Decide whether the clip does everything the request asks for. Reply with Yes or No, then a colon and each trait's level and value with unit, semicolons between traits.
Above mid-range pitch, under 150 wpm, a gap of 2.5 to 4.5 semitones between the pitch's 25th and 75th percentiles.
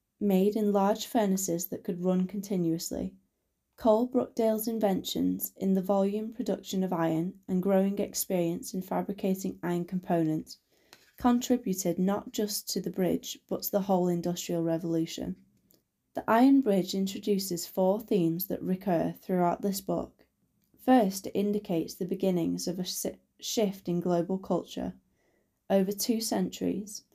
Yes: high, 195 Hz; slow, 135 wpm; average, 2.9 semitones